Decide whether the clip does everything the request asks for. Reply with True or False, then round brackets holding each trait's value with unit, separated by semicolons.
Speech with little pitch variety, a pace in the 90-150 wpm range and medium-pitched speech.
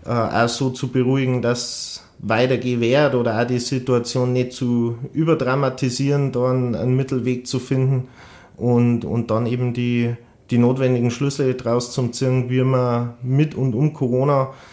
False (1.6 semitones; 145 wpm; 125 Hz)